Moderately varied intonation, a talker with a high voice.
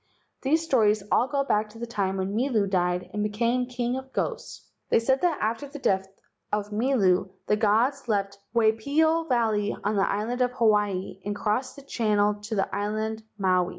Yes: average, 3.5 semitones; high, 215 Hz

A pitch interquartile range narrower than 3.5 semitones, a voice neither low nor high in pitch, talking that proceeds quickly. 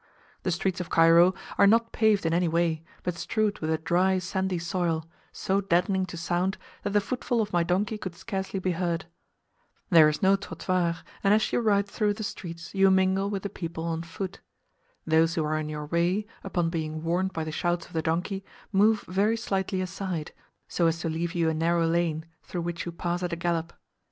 Yes: narrow, 2.6 semitones; medium, 175 Hz; fast, 210 wpm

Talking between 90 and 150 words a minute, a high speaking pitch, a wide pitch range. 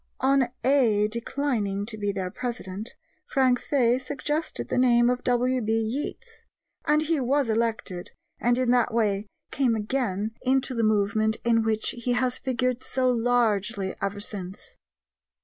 No: average, 145 wpm; high, 235 Hz; average, 3.1 semitones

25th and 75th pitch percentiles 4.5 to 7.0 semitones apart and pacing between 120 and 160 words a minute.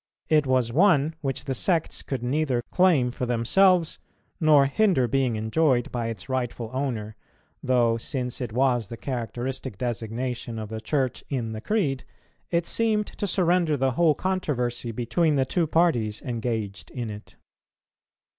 Yes: average, 4.9 semitones; average, 150 wpm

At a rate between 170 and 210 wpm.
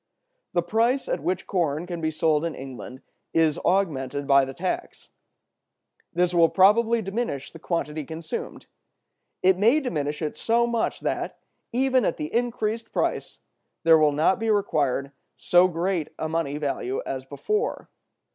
No: average, 150 wpm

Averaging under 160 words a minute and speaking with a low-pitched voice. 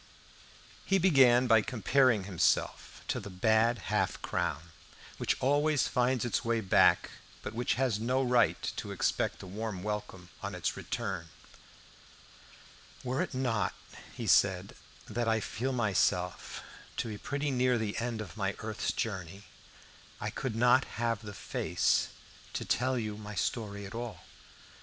Yes: average, 145 wpm; low, 115 Hz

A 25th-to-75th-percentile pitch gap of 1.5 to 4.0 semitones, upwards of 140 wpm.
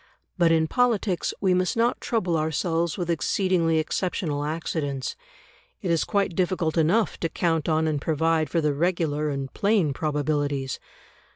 Yes: average, 3.1 semitones; average, 150 wpm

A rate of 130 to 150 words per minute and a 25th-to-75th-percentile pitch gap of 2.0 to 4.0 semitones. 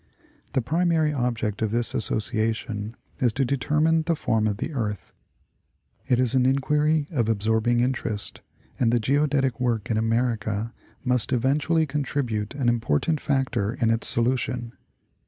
Yes: average, 140 wpm; average, 3.7 semitones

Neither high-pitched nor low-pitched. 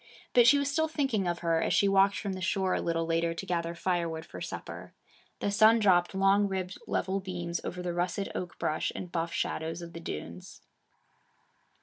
Yes: medium, 180 Hz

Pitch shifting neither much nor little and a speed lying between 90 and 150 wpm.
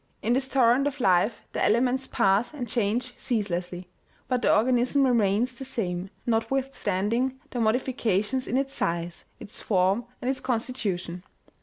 Yes: average, 4.5 semitones; average, 145 wpm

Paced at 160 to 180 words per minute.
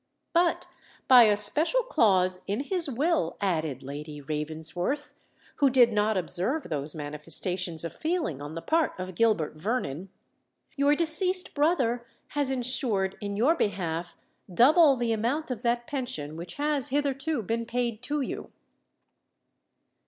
No: slow, 135 wpm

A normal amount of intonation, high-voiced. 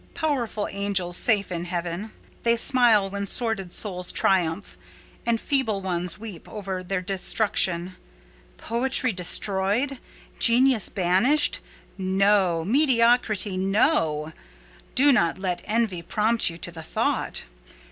Yes: average, 4.4 semitones; high, 200 Hz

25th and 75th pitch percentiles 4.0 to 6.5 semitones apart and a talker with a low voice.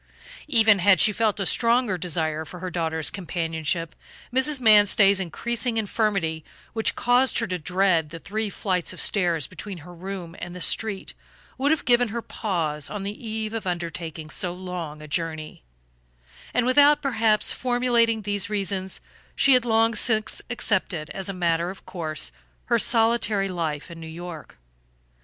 No: average, 4.9 semitones; high, 195 Hz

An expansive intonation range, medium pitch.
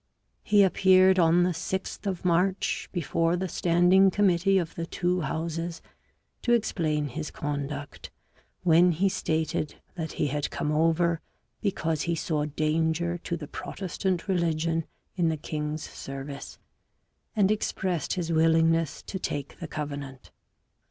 No: average, 2.9 semitones; medium, 165 Hz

